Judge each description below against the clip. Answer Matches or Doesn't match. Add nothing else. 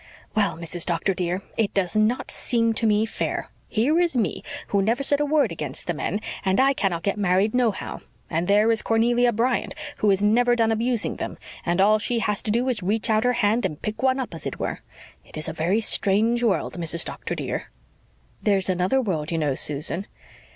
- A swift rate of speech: Matches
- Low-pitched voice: Doesn't match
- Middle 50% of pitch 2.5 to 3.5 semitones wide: Doesn't match